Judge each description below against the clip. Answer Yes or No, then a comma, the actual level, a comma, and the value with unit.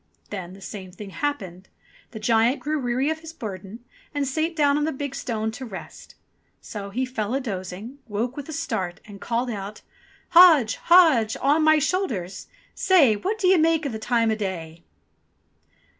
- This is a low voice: No, high, 240 Hz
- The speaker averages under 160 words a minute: No, average, 175 wpm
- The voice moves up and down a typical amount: No, wide, 6.5 semitones